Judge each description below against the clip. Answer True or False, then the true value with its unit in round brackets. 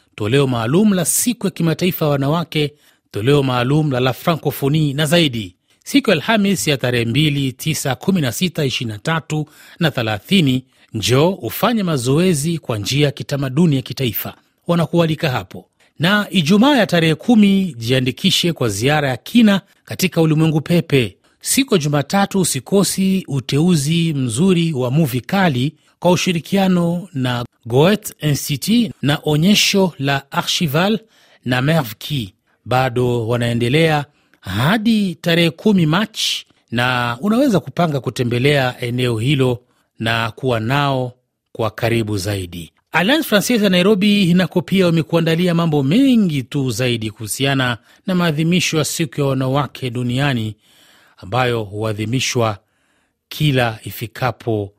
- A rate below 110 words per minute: False (115 wpm)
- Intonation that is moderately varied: False (5.8 semitones)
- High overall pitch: False (145 Hz)